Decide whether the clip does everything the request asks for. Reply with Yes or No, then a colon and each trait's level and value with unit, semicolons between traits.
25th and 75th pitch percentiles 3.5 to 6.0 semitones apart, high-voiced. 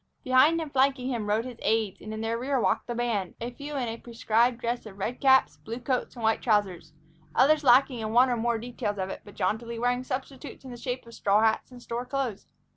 No: narrow, 2.6 semitones; high, 240 Hz